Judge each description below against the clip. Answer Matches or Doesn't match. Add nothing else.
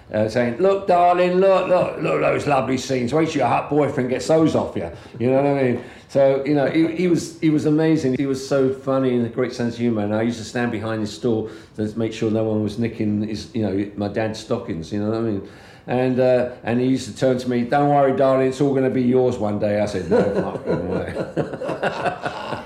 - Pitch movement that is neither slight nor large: Matches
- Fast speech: Matches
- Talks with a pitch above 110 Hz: Matches